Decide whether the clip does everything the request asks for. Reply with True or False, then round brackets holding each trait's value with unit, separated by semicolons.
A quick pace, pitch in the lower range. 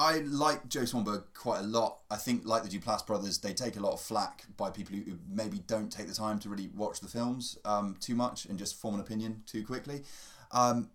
True (235 wpm; 110 Hz)